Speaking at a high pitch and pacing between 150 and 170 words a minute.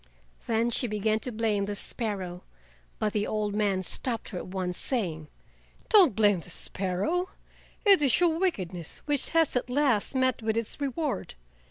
Yes: high, 220 Hz; average, 165 wpm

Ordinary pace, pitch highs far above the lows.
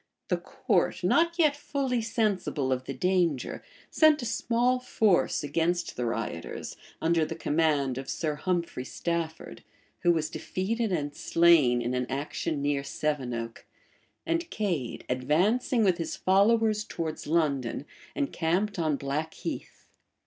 No: slow, 130 wpm; wide, 7.3 semitones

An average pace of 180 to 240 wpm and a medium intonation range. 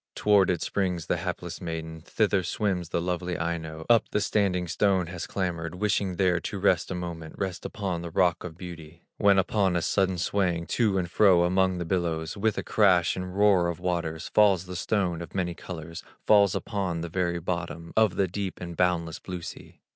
No: average, 195 wpm; narrow, 2.2 semitones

